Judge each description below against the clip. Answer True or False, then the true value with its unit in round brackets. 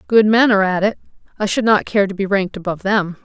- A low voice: False (200 Hz)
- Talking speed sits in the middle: False (260 wpm)